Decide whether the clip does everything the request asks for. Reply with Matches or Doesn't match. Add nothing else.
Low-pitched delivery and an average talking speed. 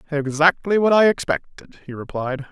Doesn't match